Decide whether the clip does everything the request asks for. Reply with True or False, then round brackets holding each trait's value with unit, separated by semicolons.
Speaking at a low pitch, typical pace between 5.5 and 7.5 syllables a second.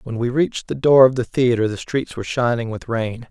True (120 Hz; 5.6 syllables/s)